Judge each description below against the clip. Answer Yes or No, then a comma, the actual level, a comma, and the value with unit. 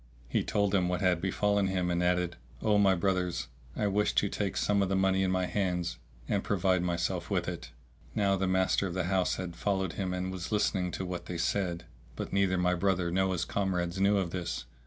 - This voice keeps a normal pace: No, fast, 220 wpm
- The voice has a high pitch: No, very low, 95 Hz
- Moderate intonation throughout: No, narrow, 1.7 semitones